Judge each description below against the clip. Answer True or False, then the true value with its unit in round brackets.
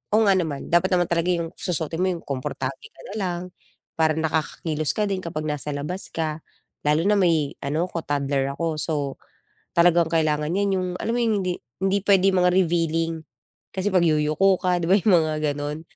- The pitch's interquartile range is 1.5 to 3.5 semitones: True (3.2 semitones)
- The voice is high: False (165 Hz)